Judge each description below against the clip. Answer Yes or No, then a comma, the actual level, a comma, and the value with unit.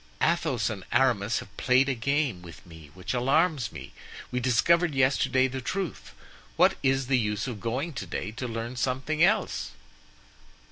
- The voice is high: No, low, 130 Hz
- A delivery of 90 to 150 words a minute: No, average, 160 wpm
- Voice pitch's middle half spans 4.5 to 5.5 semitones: No, average, 3.3 semitones